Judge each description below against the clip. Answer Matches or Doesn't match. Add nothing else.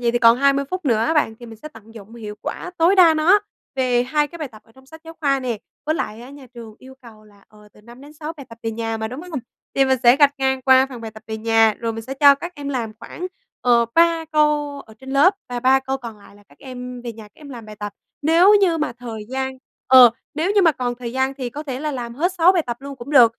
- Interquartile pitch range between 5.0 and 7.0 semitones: Doesn't match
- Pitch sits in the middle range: Doesn't match